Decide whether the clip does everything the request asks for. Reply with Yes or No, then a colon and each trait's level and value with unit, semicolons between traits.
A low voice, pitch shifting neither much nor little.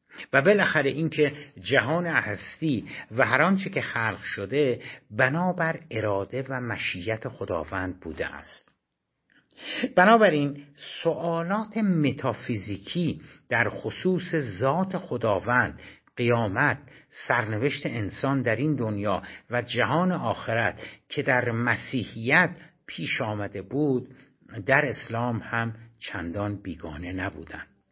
No: low, 130 Hz; wide, 5.8 semitones